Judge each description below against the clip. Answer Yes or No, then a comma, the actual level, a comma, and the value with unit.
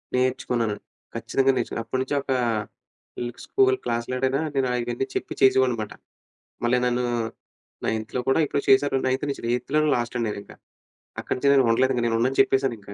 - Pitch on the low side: Yes, low, 130 Hz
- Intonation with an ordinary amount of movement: No, narrow, 2.1 semitones